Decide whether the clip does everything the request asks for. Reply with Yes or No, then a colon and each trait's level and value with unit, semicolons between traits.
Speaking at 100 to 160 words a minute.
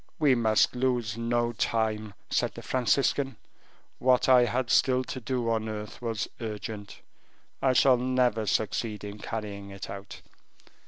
Yes: average, 145 wpm